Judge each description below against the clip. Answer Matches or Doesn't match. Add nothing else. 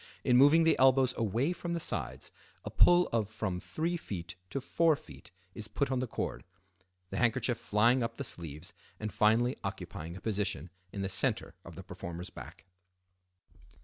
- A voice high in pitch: Doesn't match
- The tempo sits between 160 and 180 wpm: Matches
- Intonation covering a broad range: Matches